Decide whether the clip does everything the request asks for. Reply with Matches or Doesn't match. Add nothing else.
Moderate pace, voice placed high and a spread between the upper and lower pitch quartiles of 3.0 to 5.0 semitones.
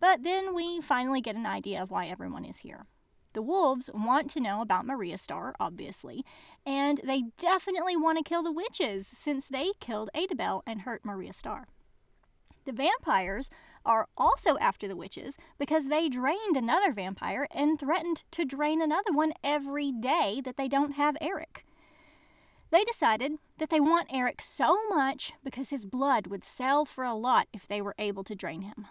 Matches